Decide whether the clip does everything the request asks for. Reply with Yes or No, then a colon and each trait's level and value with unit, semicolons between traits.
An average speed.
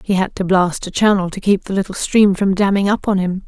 No: fast, 275 wpm